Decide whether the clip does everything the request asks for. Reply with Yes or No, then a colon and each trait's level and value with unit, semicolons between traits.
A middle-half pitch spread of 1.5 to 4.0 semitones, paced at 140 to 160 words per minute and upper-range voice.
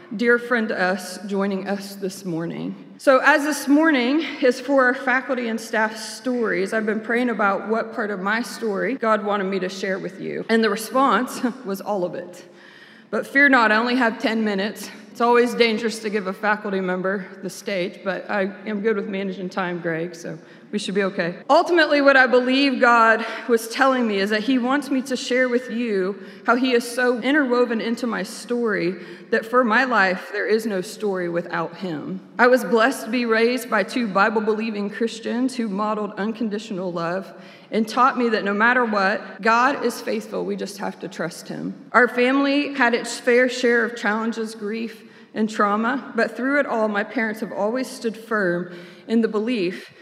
No: average, 3.7 semitones; average, 195 wpm; high, 225 Hz